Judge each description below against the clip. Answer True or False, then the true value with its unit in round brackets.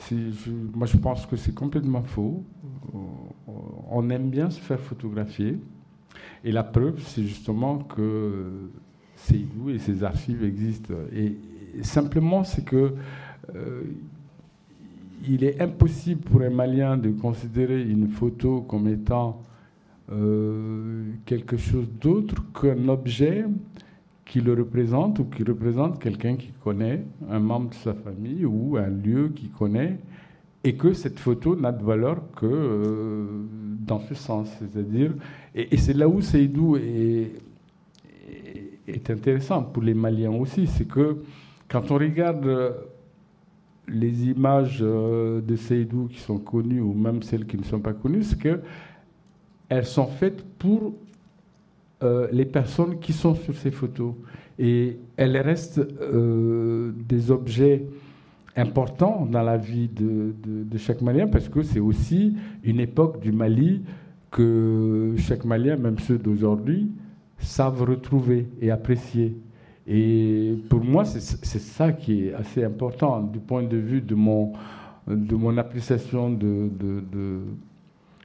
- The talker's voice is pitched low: True (120 Hz)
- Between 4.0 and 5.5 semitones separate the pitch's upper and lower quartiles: True (4.7 semitones)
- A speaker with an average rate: False (135 wpm)